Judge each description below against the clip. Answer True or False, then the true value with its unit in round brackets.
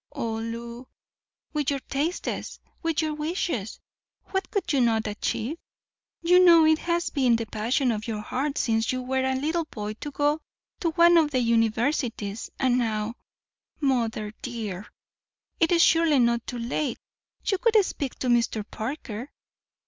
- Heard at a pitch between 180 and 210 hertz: False (255 Hz)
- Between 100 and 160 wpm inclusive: True (155 wpm)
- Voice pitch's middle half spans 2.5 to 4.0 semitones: False (5.4 semitones)